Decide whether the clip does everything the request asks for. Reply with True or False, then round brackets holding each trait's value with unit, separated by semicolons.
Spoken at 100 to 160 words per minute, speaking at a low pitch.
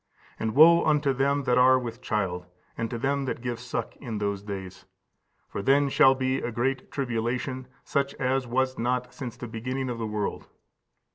False (180 wpm; 125 Hz)